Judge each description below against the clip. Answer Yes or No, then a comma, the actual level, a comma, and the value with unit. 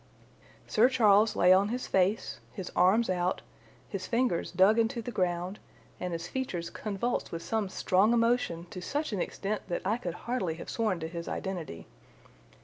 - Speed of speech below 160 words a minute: No, average, 170 wpm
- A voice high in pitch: Yes, high, 195 Hz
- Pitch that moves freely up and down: No, average, 4.4 semitones